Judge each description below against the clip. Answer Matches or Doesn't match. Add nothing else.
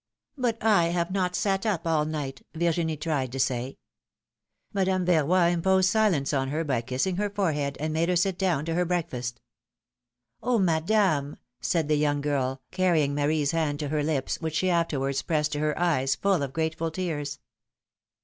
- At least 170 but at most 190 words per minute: Matches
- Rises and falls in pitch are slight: Doesn't match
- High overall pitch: Doesn't match